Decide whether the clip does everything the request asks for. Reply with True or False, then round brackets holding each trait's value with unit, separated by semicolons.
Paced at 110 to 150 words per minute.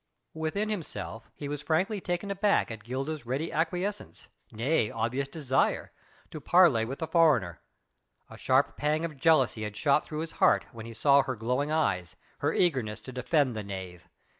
False (170 wpm)